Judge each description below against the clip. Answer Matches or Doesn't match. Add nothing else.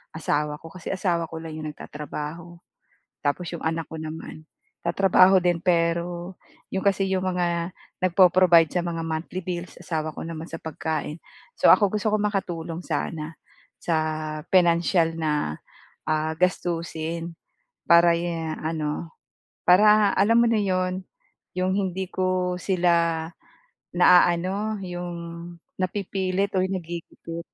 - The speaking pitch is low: Doesn't match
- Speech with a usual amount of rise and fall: Doesn't match